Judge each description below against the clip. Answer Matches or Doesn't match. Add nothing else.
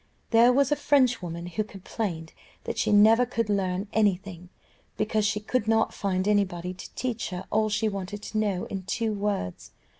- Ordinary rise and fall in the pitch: Matches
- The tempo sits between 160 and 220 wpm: Matches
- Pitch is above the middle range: Matches